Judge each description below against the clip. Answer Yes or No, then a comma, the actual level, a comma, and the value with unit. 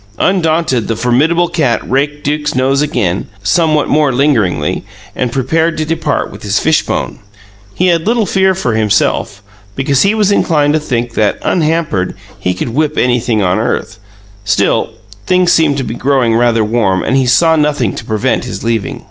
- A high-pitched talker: No, medium, 140 Hz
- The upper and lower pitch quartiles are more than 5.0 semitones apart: Yes, wide, 5.6 semitones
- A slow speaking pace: No, average, 170 wpm